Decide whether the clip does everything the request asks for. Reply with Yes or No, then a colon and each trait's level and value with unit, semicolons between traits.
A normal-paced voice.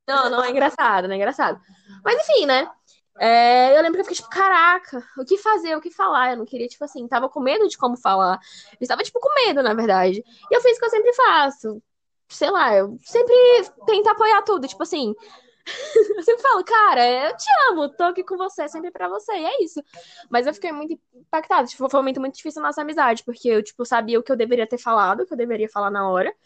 No: fast, 240 wpm